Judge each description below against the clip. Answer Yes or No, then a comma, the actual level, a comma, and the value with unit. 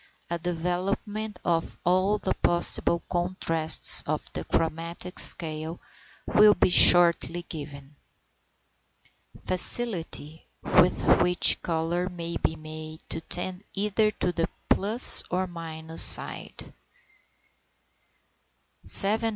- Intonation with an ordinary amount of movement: No, narrow, 2.3 semitones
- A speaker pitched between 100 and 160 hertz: No, medium, 175 Hz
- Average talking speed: No, slow, 95 wpm